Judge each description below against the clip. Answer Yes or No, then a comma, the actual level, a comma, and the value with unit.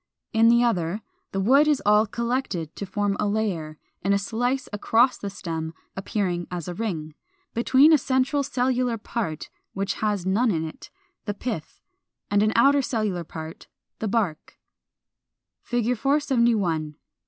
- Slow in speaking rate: No, average, 155 wpm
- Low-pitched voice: No, high, 210 Hz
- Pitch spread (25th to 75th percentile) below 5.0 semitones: No, average, 5.3 semitones